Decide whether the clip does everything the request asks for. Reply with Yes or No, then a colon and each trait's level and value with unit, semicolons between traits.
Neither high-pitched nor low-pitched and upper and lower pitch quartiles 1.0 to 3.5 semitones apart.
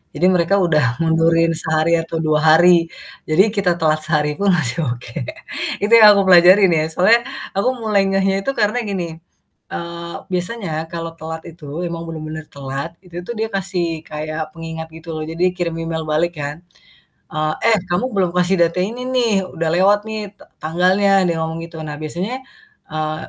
Yes: medium, 170 Hz; average, 3.1 semitones